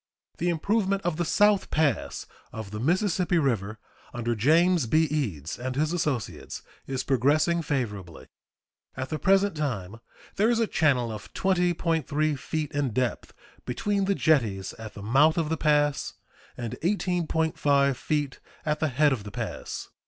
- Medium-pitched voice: Yes, medium, 150 Hz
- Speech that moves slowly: No, average, 150 wpm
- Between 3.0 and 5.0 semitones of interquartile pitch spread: No, wide, 5.6 semitones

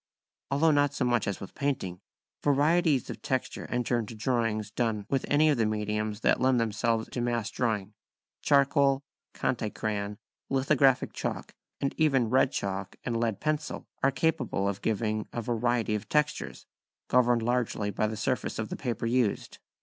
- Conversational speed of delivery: Yes, average, 165 wpm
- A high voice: No, low, 120 Hz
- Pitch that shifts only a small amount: No, average, 4.1 semitones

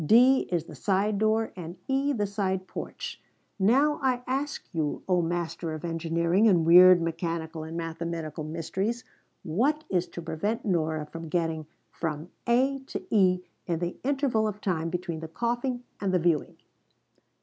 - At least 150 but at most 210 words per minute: Yes, average, 160 wpm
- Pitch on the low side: No, medium, 180 Hz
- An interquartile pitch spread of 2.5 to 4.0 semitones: No, average, 5.3 semitones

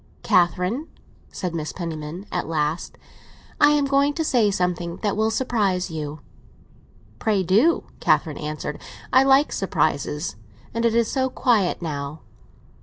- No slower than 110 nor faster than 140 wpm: Yes, slow, 135 wpm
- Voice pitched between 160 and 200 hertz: Yes, medium, 185 Hz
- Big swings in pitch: Yes, wide, 7.0 semitones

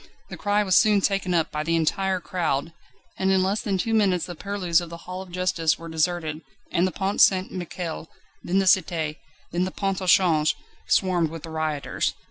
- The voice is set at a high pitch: No, medium, 180 Hz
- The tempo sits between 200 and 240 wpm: Yes, fast, 205 wpm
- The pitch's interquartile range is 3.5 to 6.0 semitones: No, average, 2.7 semitones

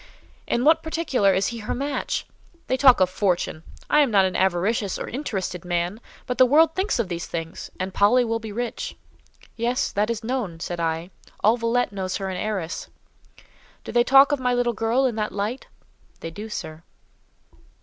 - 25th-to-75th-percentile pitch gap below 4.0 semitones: No, average, 5.0 semitones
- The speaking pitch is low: No, high, 220 Hz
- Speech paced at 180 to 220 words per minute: Yes, average, 190 wpm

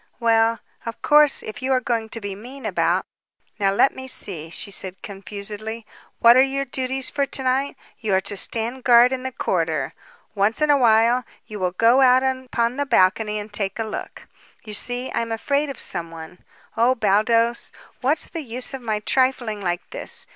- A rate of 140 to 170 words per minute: No, average, 190 wpm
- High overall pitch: Yes, high, 230 Hz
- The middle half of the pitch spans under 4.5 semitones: Yes, average, 3.9 semitones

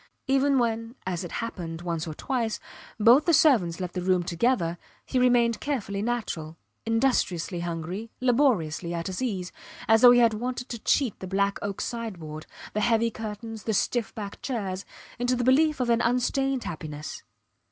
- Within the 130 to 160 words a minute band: No, average, 170 wpm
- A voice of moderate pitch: No, high, 220 Hz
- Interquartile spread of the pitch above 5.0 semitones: Yes, wide, 5.5 semitones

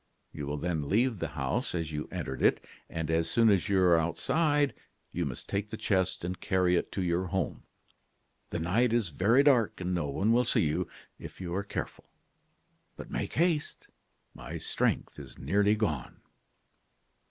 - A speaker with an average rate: Yes, average, 175 wpm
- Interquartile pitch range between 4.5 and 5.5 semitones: Yes, average, 5.0 semitones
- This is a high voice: No, very low, 95 Hz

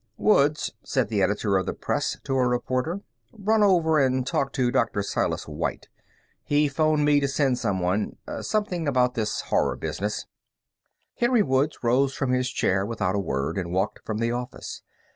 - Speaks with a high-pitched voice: No, low, 130 Hz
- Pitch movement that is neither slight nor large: No, wide, 5.9 semitones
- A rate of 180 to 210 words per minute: No, average, 170 wpm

